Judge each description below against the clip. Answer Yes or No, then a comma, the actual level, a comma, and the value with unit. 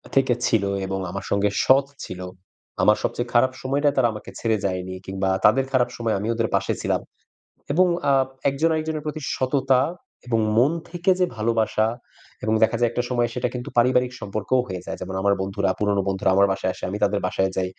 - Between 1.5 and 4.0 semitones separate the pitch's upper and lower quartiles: No, average, 4.8 semitones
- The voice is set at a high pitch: No, low, 115 Hz